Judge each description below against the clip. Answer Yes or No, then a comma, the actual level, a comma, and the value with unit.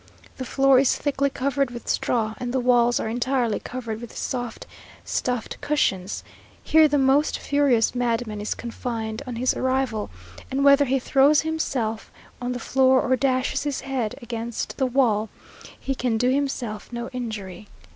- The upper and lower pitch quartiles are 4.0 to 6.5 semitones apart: No, average, 2.8 semitones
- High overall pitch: Yes, very high, 250 Hz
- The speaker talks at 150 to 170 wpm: Yes, average, 160 wpm